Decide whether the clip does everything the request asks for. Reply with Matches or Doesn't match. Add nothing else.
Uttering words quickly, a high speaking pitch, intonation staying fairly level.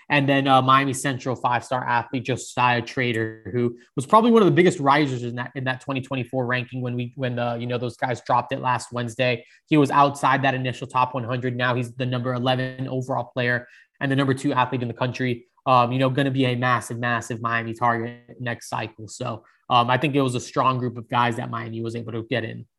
Doesn't match